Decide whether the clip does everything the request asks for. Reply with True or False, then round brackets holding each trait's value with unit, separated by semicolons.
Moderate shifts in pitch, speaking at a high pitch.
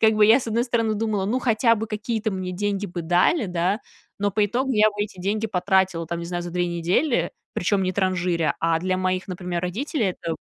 True (3.5 semitones; 195 Hz)